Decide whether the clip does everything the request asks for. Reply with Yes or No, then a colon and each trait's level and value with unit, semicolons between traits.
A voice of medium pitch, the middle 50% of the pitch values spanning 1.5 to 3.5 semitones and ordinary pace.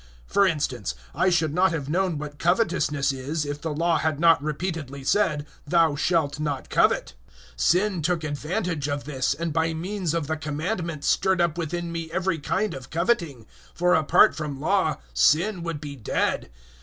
Yes: medium, 160 Hz; average, 3.2 semitones; average, 175 wpm